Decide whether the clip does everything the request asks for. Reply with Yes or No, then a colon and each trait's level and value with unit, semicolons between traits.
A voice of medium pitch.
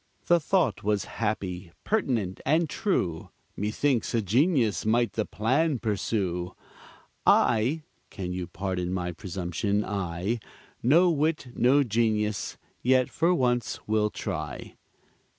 No: low, 110 Hz